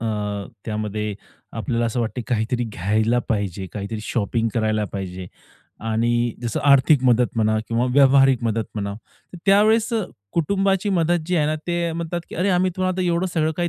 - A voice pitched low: Yes, low, 120 Hz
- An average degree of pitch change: No, wide, 7.6 semitones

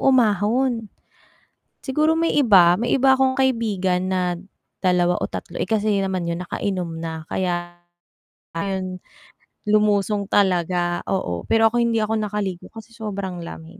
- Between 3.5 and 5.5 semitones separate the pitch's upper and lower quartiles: Yes, average, 3.9 semitones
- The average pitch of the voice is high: Yes, high, 200 Hz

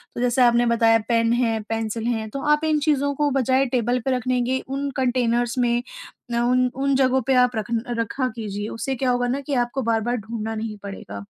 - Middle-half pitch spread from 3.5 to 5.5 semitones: No, narrow, 2.4 semitones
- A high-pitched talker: Yes, high, 245 Hz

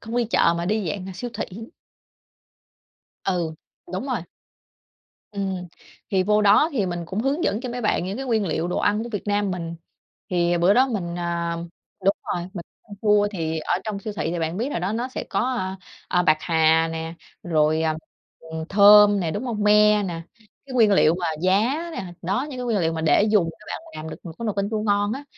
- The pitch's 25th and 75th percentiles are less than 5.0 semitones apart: Yes, average, 3.9 semitones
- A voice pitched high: Yes, high, 195 Hz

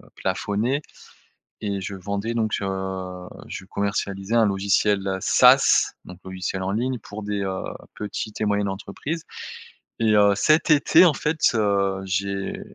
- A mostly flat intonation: Yes, narrow, 2.2 semitones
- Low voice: Yes, low, 100 Hz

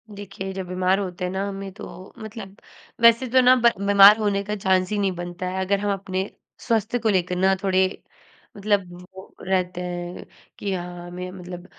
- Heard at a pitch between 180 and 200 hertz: Yes, high, 190 Hz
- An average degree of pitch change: No, narrow, 2.0 semitones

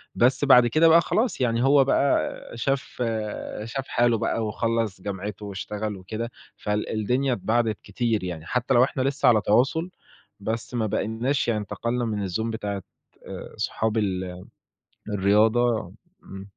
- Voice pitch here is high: No, low, 115 Hz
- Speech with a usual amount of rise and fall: Yes, average, 3.2 semitones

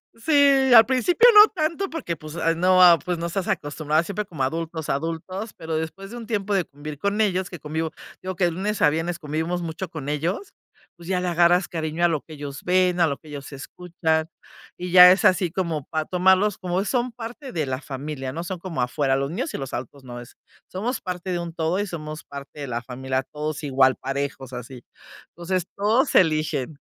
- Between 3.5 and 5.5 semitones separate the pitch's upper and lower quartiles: Yes, average, 4.0 semitones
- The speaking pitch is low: No, medium, 170 Hz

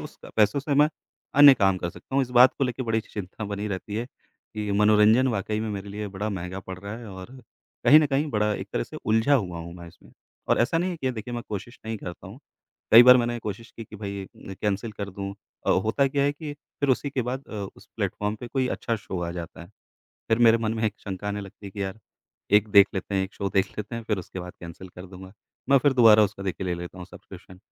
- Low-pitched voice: Yes, low, 105 Hz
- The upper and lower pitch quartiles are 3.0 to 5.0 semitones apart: Yes, average, 3.9 semitones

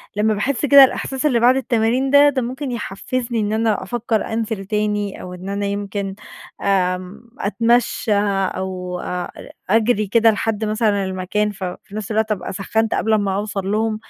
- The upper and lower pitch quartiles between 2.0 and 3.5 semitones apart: Yes, average, 2.9 semitones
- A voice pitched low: No, high, 215 Hz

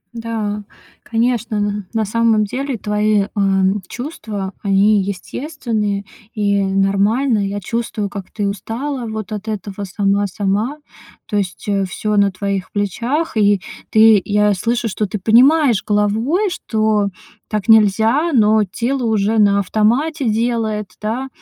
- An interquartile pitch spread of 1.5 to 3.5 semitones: Yes, narrow, 2.4 semitones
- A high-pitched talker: Yes, high, 215 Hz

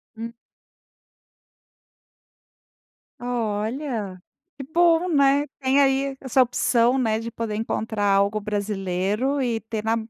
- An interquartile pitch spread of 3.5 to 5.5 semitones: Yes, average, 4.1 semitones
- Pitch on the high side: Yes, high, 230 Hz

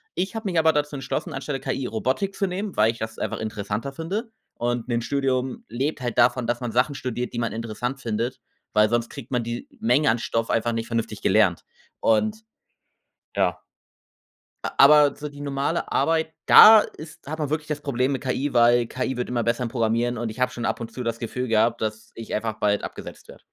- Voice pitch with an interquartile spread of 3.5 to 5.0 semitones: Yes, average, 3.9 semitones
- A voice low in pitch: Yes, low, 125 Hz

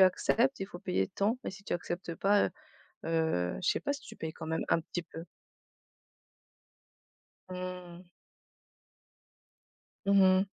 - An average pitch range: Yes, average, 3.2 semitones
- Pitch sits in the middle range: Yes, medium, 180 Hz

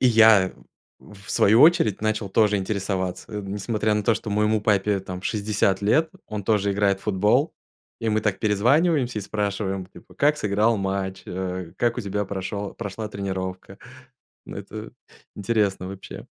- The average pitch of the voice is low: Yes, low, 105 Hz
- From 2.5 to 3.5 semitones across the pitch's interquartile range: No, narrow, 2.1 semitones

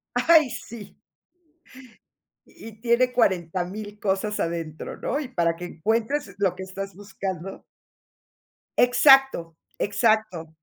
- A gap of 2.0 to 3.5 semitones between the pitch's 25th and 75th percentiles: No, average, 4.7 semitones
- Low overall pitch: No, high, 205 Hz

